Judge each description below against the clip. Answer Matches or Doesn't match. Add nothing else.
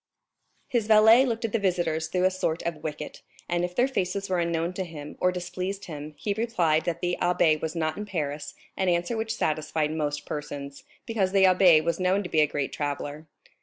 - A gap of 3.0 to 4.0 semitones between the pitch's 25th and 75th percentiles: Matches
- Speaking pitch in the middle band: Matches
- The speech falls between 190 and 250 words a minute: Matches